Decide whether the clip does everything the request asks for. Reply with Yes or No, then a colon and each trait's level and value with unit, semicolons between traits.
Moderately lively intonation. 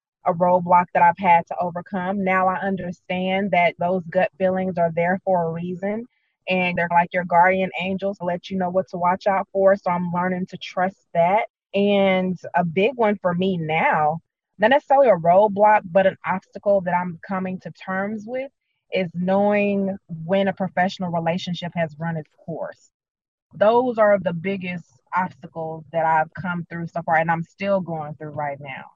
No: narrow, 2.1 semitones